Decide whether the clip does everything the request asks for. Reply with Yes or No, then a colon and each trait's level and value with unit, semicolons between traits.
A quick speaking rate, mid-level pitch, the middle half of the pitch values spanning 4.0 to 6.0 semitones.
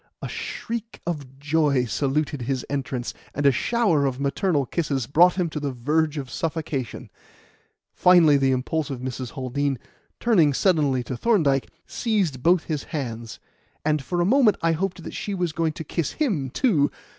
No: average, 165 wpm; medium, 150 Hz; average, 4.4 semitones